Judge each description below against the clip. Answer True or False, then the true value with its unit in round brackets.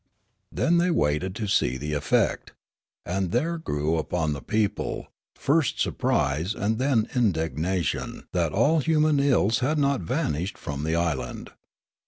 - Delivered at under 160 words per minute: True (140 wpm)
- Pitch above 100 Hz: False (95 Hz)